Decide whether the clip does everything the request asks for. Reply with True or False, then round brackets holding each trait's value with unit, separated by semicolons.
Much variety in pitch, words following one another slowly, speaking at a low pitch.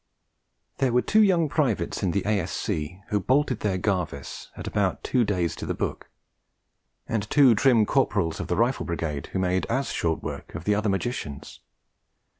False (5.8 semitones; 175 wpm; 100 Hz)